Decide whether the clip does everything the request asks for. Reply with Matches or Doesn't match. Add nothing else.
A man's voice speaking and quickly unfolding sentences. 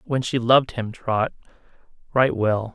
Doesn't match